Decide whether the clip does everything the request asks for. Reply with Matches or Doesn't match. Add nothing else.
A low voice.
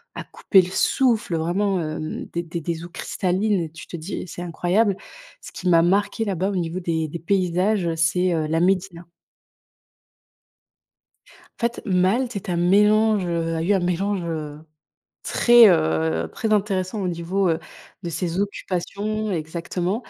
Doesn't match